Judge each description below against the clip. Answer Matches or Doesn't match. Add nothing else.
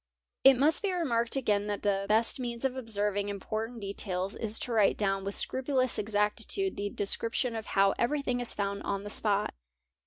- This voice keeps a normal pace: Matches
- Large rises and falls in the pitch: Doesn't match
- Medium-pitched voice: Doesn't match